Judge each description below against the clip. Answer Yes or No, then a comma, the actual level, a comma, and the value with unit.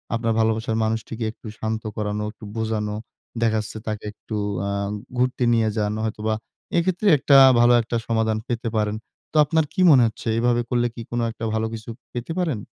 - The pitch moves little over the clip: Yes, narrow, 1.7 semitones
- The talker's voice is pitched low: Yes, low, 110 Hz